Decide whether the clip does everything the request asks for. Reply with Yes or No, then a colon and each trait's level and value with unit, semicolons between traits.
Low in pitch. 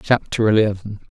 Yes: low, 105 Hz